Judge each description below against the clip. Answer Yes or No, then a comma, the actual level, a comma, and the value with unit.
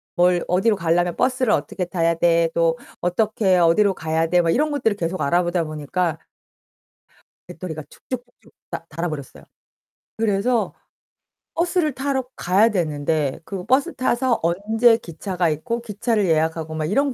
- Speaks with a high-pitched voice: No, medium, 180 Hz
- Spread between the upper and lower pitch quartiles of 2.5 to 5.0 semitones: No, wide, 5.6 semitones